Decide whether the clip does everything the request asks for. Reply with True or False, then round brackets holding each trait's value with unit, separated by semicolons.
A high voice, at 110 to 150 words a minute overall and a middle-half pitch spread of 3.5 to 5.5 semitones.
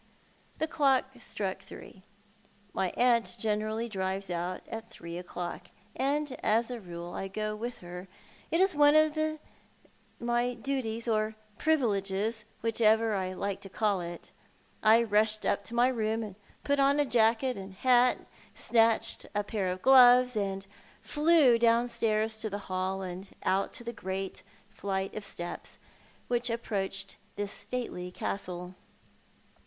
True (220 Hz; 140 wpm; 3.9 semitones)